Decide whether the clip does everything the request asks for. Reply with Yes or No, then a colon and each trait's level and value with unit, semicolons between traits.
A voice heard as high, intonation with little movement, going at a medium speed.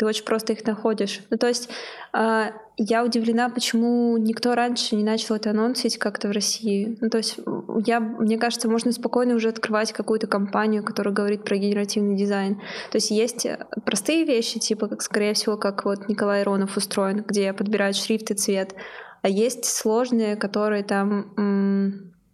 No: high, 220 Hz; narrow, 2.1 semitones; fast, 170 wpm